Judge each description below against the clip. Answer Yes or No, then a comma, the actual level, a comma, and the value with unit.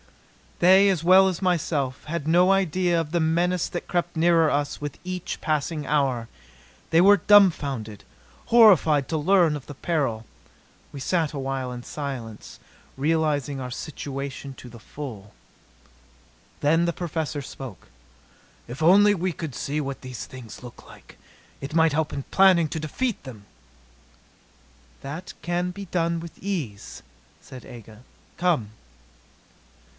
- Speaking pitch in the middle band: Yes, medium, 155 Hz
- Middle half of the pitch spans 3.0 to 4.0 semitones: No, average, 4.5 semitones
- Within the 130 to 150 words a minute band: Yes, average, 140 wpm